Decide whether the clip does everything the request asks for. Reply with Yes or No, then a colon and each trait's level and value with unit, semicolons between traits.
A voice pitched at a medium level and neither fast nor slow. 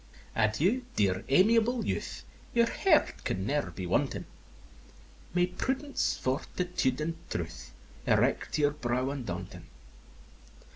No: medium, 145 Hz; slow, 110 wpm